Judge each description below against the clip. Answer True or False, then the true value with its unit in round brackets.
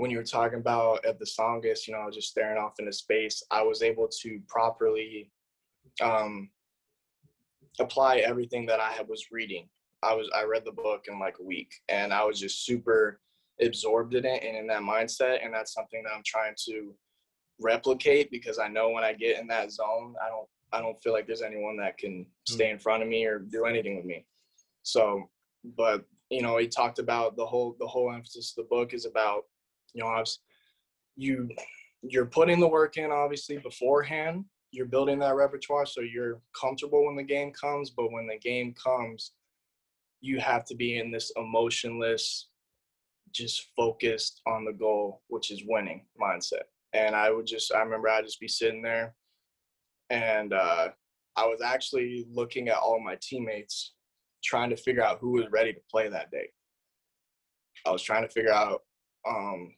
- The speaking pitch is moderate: False (115 Hz)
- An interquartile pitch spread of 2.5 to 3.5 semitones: False (3.9 semitones)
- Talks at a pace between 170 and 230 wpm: True (190 wpm)